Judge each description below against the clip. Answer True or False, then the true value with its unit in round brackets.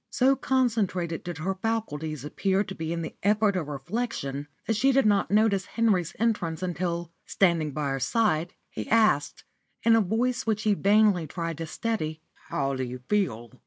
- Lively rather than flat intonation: True (5.7 semitones)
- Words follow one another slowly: False (175 wpm)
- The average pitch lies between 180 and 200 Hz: True (185 Hz)